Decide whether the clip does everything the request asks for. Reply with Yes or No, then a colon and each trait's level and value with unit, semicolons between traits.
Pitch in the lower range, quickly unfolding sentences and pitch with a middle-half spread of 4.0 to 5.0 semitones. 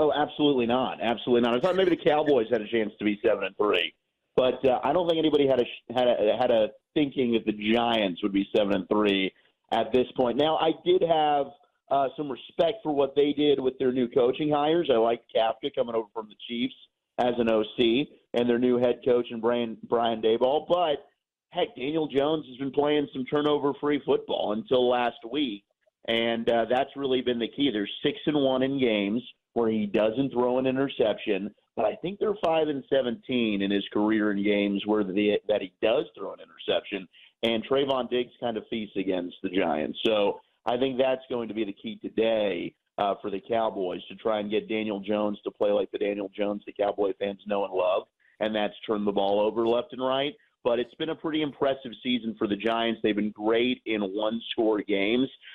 Yes: low, 120 Hz; fast, 215 wpm; average, 4.6 semitones